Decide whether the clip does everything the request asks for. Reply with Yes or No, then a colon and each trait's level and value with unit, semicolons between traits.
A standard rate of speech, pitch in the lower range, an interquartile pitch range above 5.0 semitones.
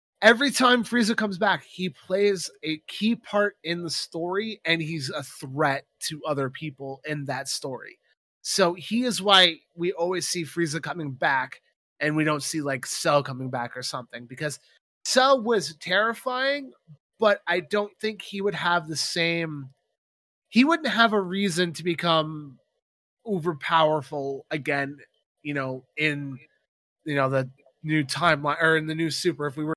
No: average, 165 wpm; medium, 160 Hz; wide, 5.4 semitones